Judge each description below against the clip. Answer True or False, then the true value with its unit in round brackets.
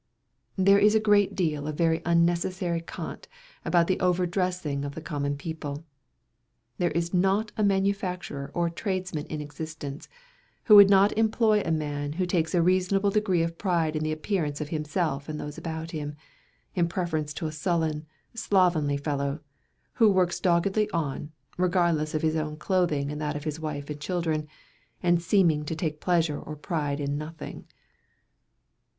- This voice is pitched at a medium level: True (165 Hz)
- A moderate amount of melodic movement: True (3.4 semitones)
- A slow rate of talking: False (165 wpm)